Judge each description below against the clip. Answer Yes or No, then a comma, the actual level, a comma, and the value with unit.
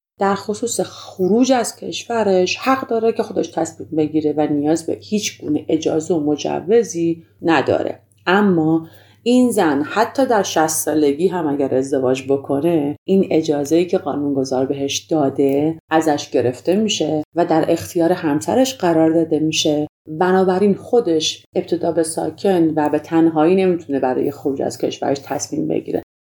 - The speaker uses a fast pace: No, average, 140 wpm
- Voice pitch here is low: No, medium, 165 Hz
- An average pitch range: Yes, average, 4.1 semitones